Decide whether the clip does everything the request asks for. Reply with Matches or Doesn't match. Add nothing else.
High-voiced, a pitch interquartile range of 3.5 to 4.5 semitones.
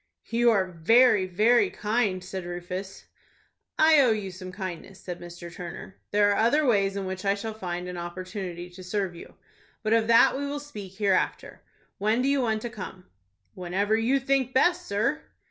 Matches